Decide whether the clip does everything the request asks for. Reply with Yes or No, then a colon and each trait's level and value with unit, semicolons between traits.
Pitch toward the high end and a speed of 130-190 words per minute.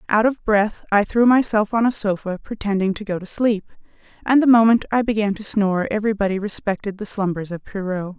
No: high, 210 Hz; average, 200 wpm